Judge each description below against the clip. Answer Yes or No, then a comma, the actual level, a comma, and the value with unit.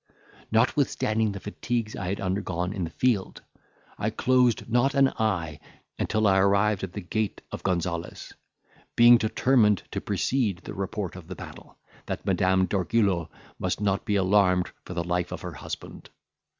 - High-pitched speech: No, low, 100 Hz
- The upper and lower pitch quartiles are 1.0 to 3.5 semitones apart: Yes, average, 3.2 semitones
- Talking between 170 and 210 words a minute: No, average, 160 wpm